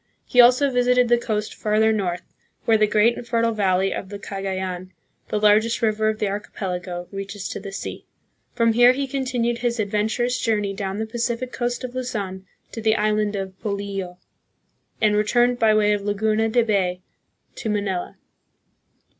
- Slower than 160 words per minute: No, average, 170 wpm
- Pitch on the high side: Yes, high, 215 Hz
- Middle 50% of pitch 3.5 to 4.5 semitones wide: No, average, 3.1 semitones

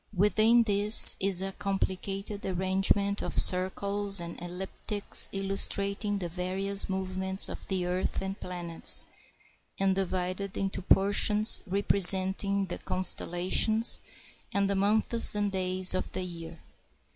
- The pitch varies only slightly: Yes, narrow, 1.4 semitones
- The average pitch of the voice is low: No, high, 195 Hz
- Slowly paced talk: Yes, slow, 120 wpm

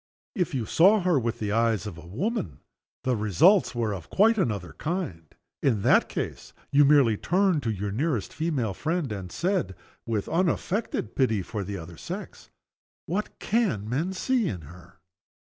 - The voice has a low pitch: Yes, low, 125 Hz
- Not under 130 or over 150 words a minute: No, average, 170 wpm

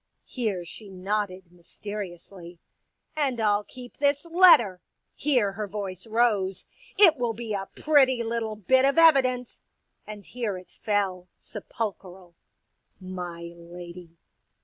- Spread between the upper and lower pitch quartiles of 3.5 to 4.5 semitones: No, average, 5.0 semitones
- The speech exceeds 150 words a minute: No, average, 140 wpm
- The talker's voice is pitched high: Yes, high, 210 Hz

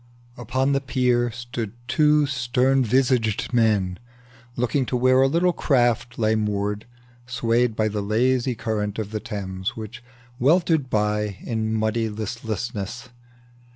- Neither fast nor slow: No, slow, 130 wpm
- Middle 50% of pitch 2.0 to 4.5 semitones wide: Yes, average, 3.0 semitones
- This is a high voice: No, low, 115 Hz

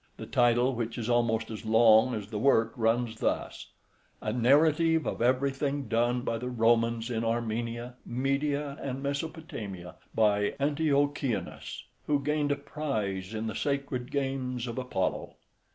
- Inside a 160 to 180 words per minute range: No, average, 140 wpm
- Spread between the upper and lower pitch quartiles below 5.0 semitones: Yes, average, 3.6 semitones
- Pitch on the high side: No, low, 120 Hz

